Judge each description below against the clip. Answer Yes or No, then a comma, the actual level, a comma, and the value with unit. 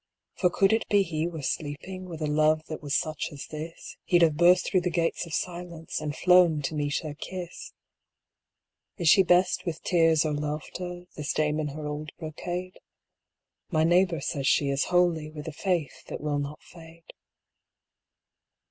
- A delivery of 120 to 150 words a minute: No, average, 175 wpm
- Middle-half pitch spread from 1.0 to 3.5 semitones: Yes, average, 2.8 semitones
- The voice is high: No, medium, 160 Hz